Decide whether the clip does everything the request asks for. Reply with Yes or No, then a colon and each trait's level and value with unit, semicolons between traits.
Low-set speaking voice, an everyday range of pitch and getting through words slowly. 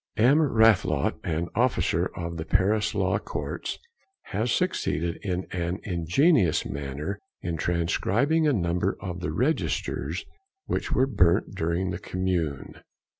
Yes: very low, 90 Hz; average, 4.4 semitones; slow, 125 wpm